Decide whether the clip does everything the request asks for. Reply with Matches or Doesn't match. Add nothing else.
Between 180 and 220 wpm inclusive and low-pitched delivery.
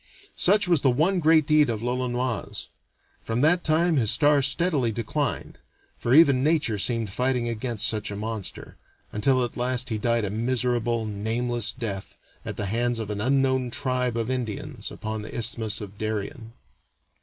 Doesn't match